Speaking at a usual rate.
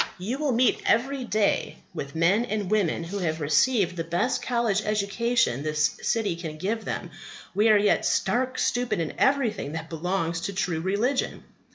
Yes: average, 170 wpm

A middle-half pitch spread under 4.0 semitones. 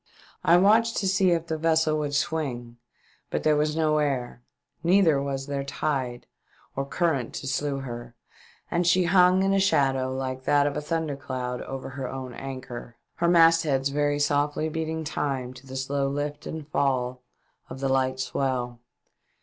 Yes: average, 3.4 semitones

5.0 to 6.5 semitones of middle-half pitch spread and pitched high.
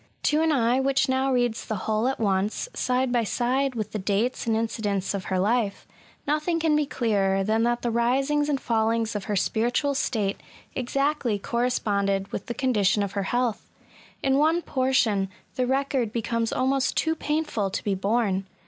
No: average, 4.3 semitones; high, 235 Hz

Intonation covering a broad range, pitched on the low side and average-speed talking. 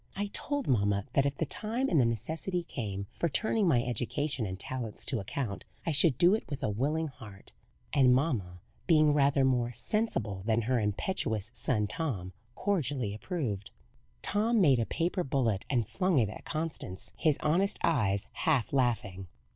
Yes: wide, 7.0 semitones; low, 130 Hz; average, 170 wpm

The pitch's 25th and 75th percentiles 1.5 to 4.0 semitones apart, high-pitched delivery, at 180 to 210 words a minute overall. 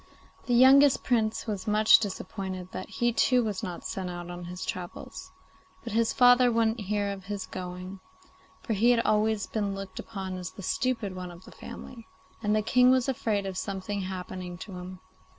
Yes: average, 3.7 semitones; high, 200 Hz; average, 185 wpm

